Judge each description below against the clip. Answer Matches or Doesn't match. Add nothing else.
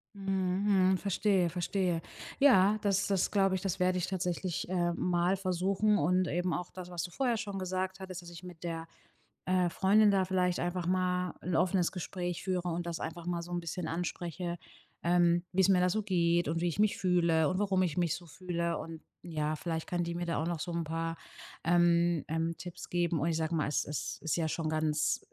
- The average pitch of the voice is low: Doesn't match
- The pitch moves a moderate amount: Doesn't match